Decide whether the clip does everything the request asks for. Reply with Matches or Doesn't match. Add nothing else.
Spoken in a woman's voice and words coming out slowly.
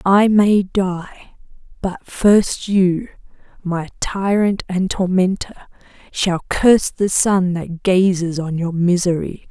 Matches